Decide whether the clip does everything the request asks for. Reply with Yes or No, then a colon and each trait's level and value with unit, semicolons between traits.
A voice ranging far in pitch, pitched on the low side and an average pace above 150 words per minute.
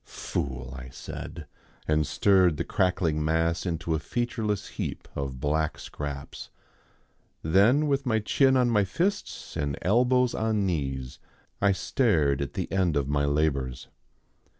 No: wide, 6.8 semitones; very low, 85 Hz; average, 140 wpm